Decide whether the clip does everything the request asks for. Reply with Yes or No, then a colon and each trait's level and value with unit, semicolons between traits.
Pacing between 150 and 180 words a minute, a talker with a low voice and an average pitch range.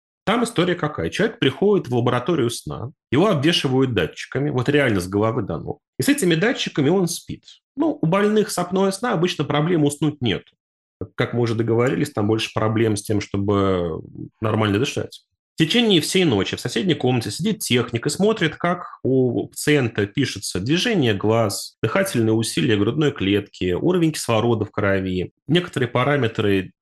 No: fast, 160 wpm; low, 130 Hz; wide, 7.4 semitones